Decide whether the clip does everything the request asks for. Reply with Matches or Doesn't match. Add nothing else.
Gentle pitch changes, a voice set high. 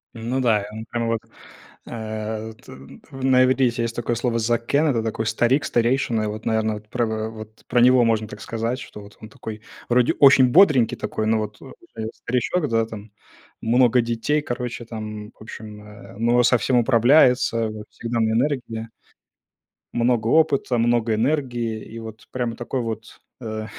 Doesn't match